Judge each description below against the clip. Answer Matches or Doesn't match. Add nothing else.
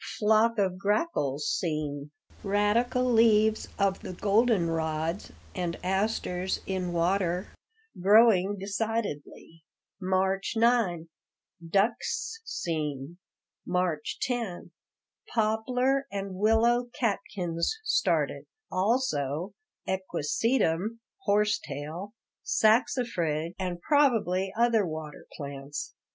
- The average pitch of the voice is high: Matches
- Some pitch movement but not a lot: Matches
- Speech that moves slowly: Matches